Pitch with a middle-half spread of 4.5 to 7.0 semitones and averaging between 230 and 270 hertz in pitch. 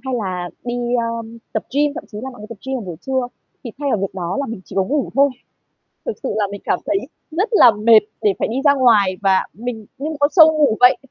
Yes: average, 4.9 semitones; high, 235 Hz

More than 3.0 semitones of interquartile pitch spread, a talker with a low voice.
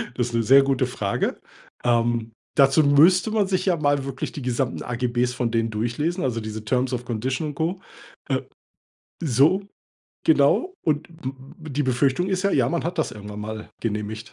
Yes: average, 4.7 semitones; low, 130 Hz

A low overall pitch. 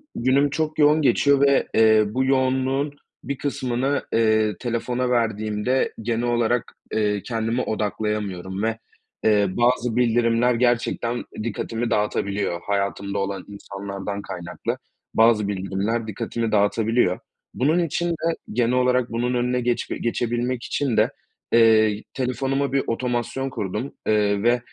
Yes: low, 115 Hz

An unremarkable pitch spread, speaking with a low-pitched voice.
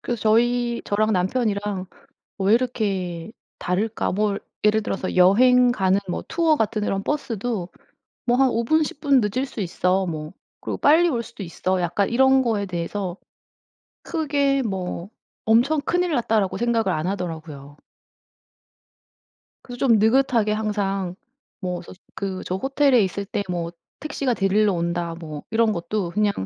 No: average, 4.8 semitones; high, 210 Hz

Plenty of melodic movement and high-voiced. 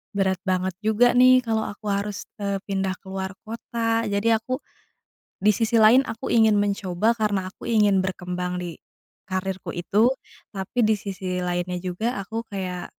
No: average, 2.9 semitones; high, 200 Hz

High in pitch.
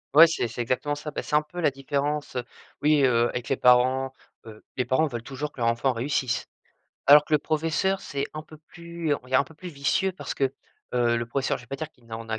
No: medium, 140 Hz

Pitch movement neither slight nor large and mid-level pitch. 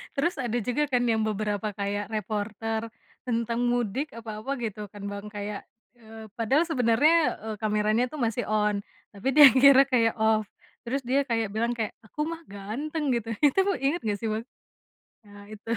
No: average, 3.0 semitones; high, 225 Hz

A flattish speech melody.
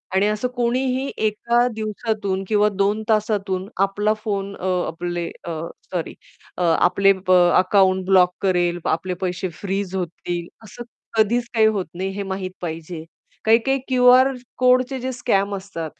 No: average, 3.2 semitones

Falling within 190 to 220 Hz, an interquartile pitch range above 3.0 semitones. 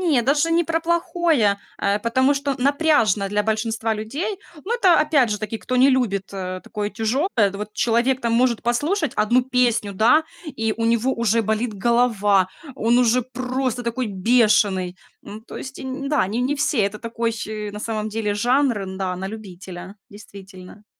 No: high, 230 Hz; average, 4.0 semitones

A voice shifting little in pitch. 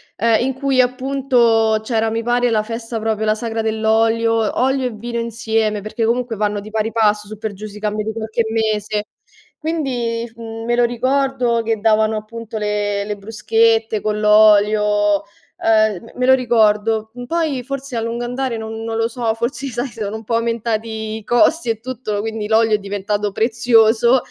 Yes: narrow, 1.8 semitones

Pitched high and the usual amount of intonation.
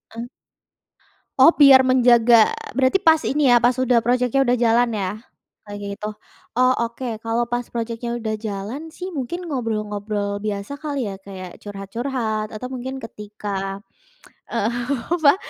Yes: high, 235 Hz; average, 3.6 semitones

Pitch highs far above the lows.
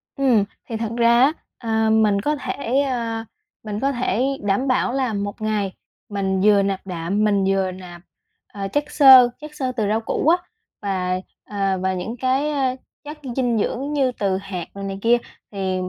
No: average, 4.6 semitones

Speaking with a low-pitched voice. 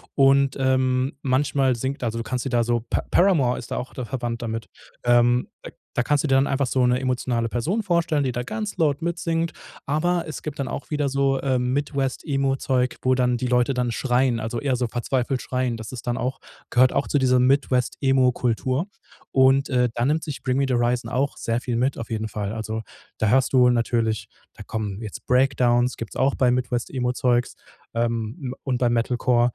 Yes: low, 125 Hz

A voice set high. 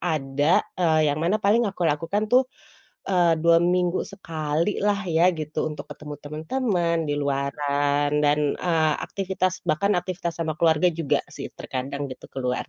No: medium, 165 Hz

